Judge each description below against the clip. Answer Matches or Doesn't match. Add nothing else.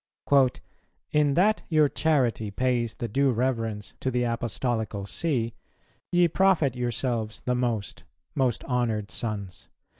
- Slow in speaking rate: Matches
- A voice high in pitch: Doesn't match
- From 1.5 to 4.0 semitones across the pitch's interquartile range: Matches